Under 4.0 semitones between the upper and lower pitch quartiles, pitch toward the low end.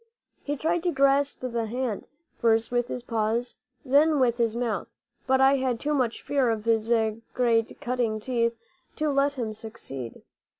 No: average, 3.3 semitones; high, 245 Hz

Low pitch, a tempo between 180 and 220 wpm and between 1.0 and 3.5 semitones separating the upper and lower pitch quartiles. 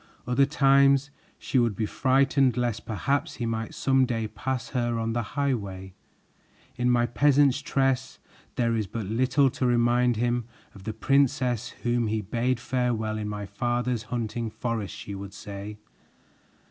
No: low, 120 Hz; average, 155 wpm; average, 2.9 semitones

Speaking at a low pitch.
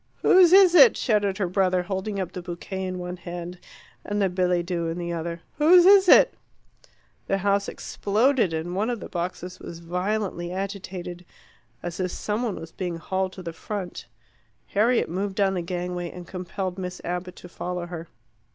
No: medium, 185 Hz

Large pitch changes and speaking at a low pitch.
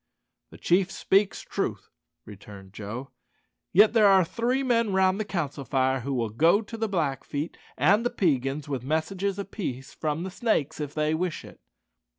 No: wide, 6.6 semitones; medium, 165 Hz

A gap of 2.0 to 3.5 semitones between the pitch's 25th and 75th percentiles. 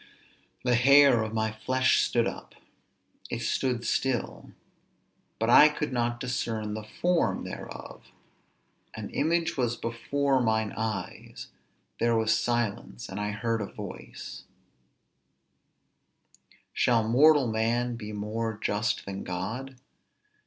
Yes: average, 2.8 semitones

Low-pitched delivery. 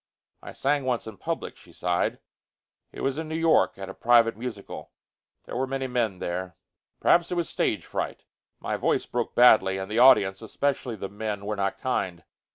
Yes: low, 115 Hz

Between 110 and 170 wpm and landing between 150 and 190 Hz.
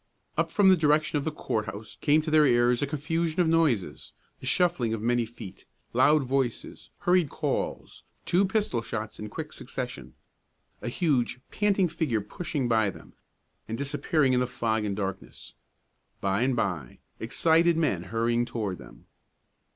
No: average, 160 wpm; low, 125 Hz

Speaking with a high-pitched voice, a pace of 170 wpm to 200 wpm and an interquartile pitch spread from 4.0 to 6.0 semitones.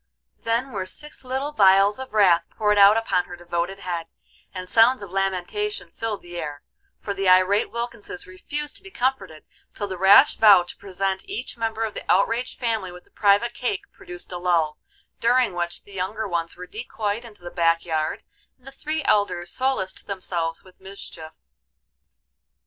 Yes: high, 195 Hz; average, 175 wpm; average, 4.3 semitones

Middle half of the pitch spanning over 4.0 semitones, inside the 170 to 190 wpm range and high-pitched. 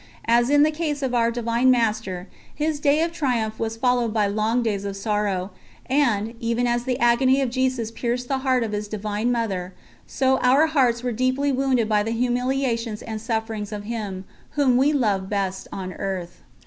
No: average, 3.5 semitones; average, 185 wpm; high, 235 Hz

